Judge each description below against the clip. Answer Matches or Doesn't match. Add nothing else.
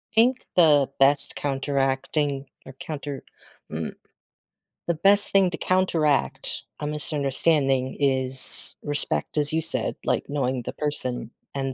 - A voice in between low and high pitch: Matches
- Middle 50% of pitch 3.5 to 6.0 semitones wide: Doesn't match